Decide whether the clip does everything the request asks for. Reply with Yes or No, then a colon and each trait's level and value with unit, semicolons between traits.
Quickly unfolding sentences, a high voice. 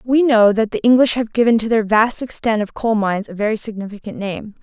Yes: fast, 235 wpm; high, 215 Hz